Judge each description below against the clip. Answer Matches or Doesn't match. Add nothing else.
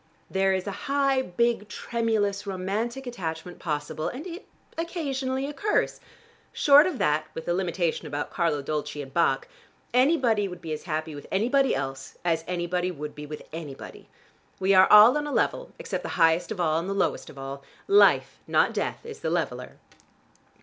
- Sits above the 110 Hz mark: Matches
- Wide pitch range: Matches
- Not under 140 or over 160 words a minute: Doesn't match